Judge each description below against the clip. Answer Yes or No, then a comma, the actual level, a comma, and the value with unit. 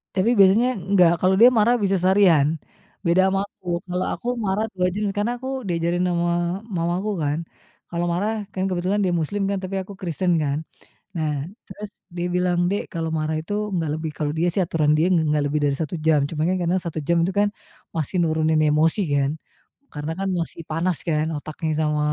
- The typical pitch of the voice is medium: Yes, medium, 175 Hz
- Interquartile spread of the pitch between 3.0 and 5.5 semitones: Yes, average, 3.3 semitones